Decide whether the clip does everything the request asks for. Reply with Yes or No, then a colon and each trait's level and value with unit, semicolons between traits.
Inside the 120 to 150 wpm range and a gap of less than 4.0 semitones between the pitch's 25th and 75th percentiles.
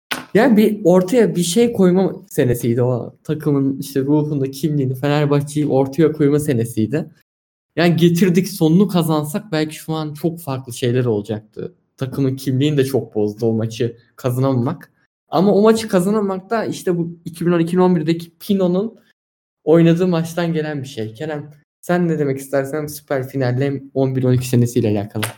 No: fast, 140 wpm; average, 4.6 semitones